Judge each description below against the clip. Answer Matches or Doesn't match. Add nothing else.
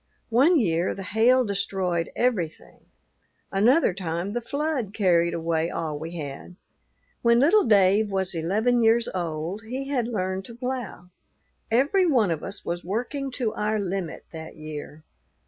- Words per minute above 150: Doesn't match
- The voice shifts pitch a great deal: Matches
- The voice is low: Doesn't match